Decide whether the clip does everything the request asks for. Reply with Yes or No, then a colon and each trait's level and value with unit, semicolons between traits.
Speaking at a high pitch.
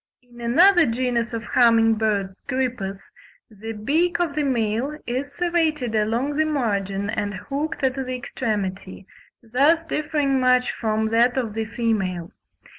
Yes: high, 240 Hz